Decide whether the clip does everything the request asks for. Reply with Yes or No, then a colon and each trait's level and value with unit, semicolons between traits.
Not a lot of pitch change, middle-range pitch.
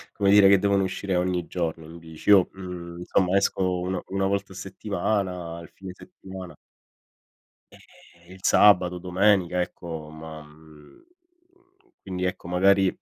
No: narrow, 2.2 semitones; very low, 90 Hz